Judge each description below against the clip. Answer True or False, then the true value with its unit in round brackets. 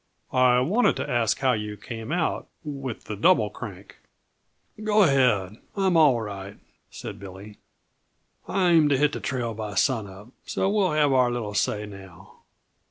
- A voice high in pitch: False (120 Hz)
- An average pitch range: False (6.1 semitones)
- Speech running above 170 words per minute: False (165 wpm)